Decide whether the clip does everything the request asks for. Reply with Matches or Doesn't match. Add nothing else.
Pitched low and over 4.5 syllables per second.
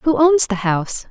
Doesn't match